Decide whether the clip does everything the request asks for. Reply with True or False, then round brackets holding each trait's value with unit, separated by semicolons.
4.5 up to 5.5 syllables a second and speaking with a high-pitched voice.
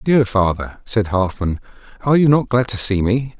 False (4.8 syllables/s; 110 Hz)